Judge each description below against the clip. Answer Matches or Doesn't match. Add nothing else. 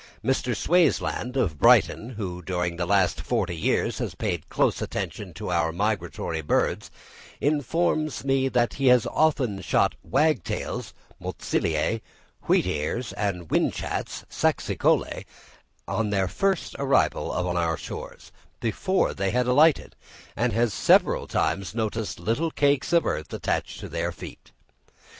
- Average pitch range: Doesn't match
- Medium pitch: Doesn't match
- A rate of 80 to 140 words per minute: Matches